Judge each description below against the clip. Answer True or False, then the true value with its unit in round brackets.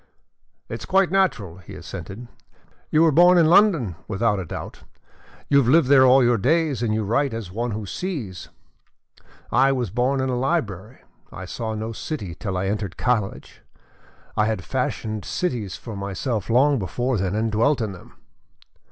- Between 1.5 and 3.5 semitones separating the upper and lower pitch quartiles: False (5.2 semitones)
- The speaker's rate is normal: True (175 wpm)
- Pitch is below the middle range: True (115 Hz)